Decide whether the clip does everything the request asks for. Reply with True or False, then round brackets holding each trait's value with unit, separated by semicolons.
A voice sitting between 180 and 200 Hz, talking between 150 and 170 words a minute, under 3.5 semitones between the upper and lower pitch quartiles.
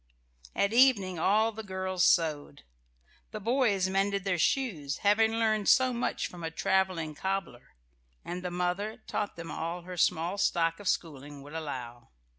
False (185 Hz; 155 wpm; 4.1 semitones)